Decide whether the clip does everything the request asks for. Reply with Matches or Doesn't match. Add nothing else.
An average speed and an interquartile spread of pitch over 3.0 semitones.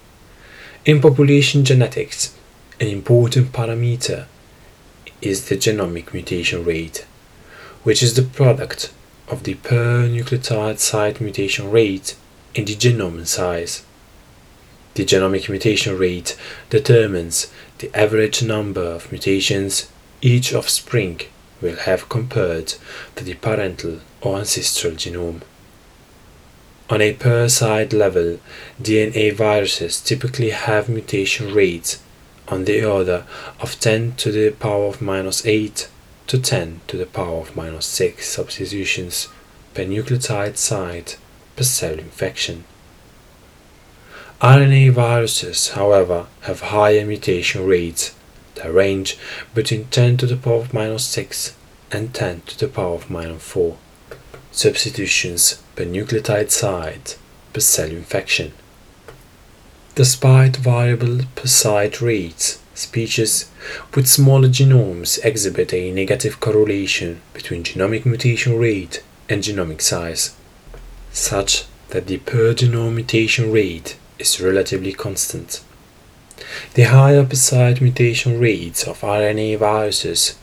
Doesn't match